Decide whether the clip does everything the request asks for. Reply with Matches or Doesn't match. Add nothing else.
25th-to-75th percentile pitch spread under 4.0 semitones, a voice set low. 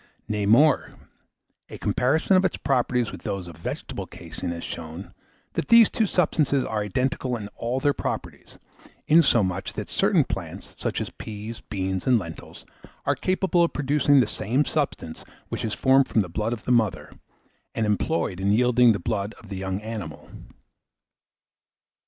Doesn't match